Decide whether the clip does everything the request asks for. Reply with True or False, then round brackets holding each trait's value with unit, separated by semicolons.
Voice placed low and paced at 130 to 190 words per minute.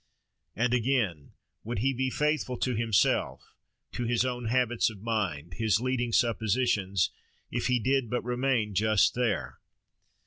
True (120 Hz; 140 wpm)